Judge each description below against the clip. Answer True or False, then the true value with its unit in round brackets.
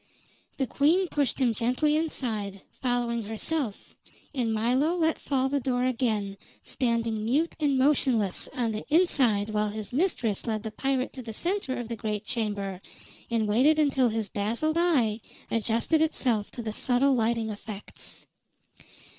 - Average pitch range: True (4.2 semitones)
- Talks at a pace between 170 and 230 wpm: False (150 wpm)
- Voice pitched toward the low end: False (240 Hz)